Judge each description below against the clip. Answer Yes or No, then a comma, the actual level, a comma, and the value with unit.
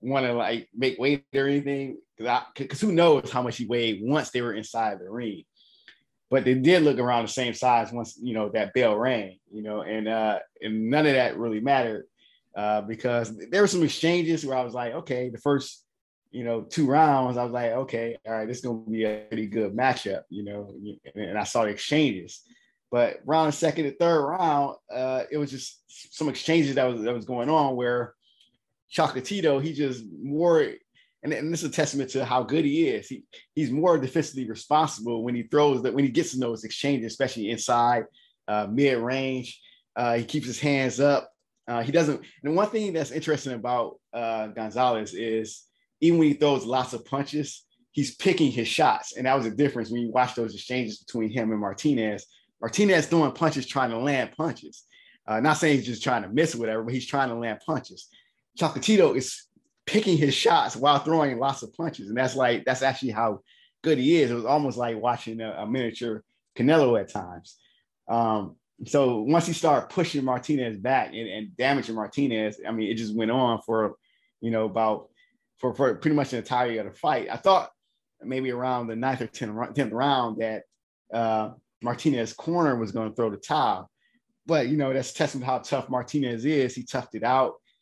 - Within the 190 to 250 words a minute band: Yes, fast, 205 wpm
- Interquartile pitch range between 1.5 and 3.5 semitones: No, average, 4.2 semitones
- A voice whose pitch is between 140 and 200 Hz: No, low, 125 Hz